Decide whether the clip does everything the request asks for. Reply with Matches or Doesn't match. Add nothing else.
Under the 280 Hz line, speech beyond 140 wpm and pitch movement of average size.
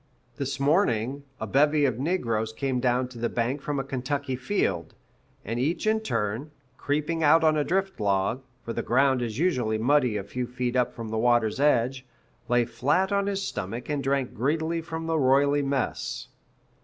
Matches